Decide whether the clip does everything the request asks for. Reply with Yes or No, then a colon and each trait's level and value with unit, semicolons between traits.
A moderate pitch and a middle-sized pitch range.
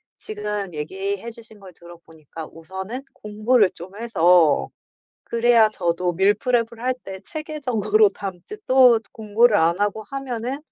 No: high, 210 Hz; average, 4.3 semitones